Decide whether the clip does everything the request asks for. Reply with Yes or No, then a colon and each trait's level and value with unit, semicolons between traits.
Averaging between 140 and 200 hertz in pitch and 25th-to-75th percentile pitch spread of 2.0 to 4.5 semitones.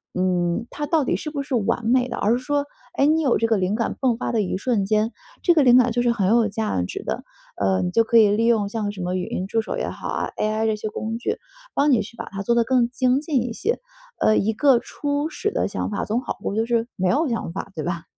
No: high, 230 Hz; average, 3.9 semitones